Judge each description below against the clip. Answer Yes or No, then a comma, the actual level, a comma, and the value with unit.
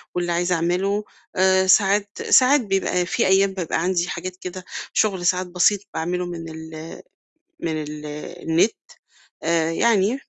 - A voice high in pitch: No, medium, 180 Hz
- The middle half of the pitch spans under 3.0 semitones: Yes, narrow, 2.4 semitones